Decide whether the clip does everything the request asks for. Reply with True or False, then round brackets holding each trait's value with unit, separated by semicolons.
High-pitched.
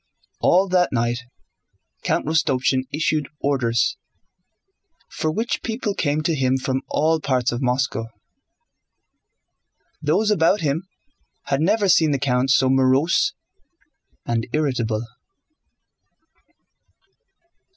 False (140 Hz)